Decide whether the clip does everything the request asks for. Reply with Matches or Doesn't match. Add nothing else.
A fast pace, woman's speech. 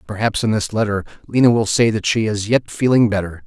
Doesn't match